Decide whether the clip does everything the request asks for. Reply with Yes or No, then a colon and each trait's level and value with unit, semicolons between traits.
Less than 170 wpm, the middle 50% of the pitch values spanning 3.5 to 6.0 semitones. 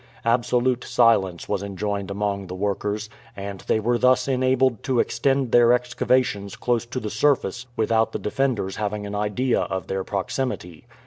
Yes: average, 155 wpm; average, 3.9 semitones